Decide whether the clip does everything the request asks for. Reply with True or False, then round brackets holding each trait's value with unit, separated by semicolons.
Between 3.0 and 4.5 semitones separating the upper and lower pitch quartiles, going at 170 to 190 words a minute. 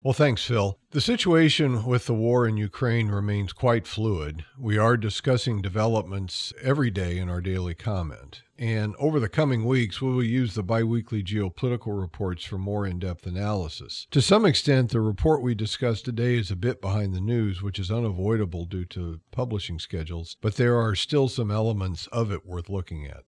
True (4.0 semitones; 185 wpm)